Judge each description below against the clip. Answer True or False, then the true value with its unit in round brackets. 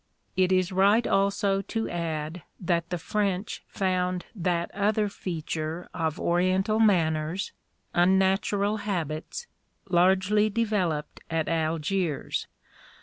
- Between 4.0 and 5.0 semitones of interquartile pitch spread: False (3.0 semitones)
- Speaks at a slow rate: True (100 wpm)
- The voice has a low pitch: False (185 Hz)